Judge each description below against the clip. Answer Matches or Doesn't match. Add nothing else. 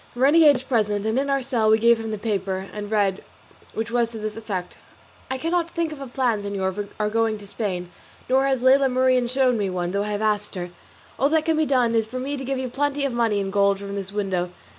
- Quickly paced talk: Matches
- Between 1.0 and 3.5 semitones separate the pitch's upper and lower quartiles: Doesn't match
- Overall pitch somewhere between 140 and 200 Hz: Doesn't match